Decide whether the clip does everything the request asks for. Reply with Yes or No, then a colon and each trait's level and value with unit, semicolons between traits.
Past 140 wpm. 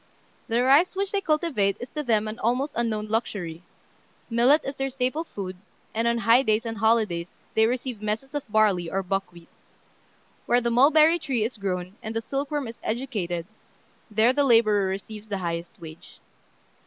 Yes: average, 170 wpm